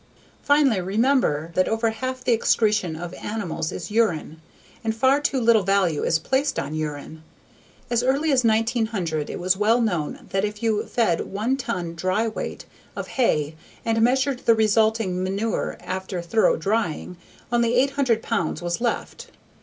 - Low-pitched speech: No, high, 220 Hz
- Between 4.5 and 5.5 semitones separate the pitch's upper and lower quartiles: Yes, average, 4.8 semitones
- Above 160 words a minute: No, average, 155 wpm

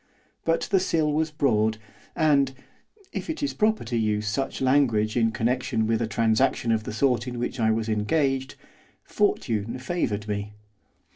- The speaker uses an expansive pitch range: No, average, 4.2 semitones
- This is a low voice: Yes, low, 120 Hz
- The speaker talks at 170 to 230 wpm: No, average, 160 wpm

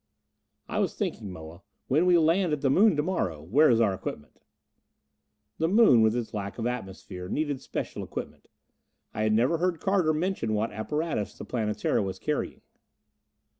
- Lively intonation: Yes, wide, 7.5 semitones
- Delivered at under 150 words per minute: No, average, 170 wpm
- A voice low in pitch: Yes, low, 125 Hz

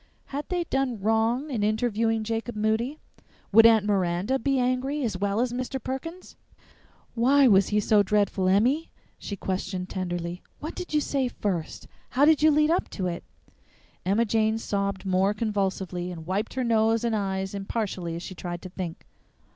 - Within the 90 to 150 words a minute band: No, average, 170 wpm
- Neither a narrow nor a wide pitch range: Yes, average, 4.7 semitones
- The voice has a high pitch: Yes, high, 215 Hz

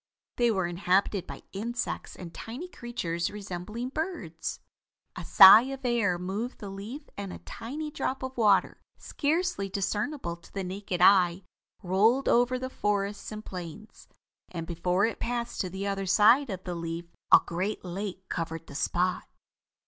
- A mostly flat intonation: No, average, 4.9 semitones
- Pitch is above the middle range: Yes, high, 200 Hz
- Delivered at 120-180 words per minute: Yes, average, 155 wpm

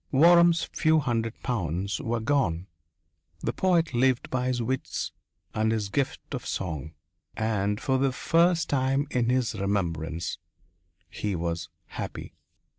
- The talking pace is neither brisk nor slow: No, slow, 130 wpm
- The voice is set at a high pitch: No, low, 120 Hz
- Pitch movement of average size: No, wide, 5.7 semitones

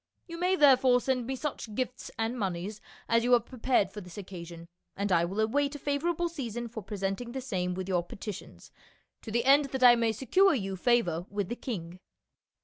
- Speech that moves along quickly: Yes, fast, 210 wpm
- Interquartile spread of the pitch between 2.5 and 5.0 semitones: No, wide, 5.4 semitones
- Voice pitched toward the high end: Yes, high, 230 Hz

